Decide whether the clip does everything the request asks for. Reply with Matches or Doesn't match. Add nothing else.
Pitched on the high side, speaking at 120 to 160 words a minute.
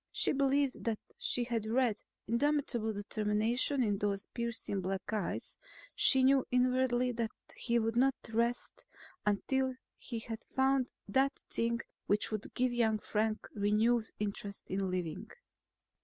Matches